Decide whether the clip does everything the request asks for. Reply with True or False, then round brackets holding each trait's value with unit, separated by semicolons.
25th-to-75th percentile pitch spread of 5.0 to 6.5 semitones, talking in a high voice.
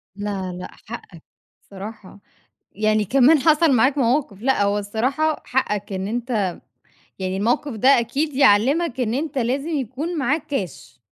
True (5.3 semitones; 240 Hz)